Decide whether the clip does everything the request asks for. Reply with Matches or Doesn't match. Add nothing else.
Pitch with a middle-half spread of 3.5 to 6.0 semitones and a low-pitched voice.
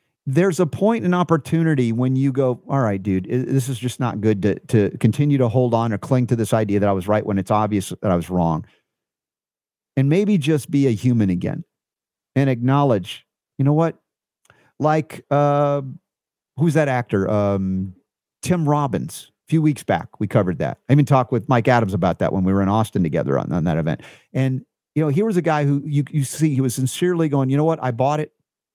Matches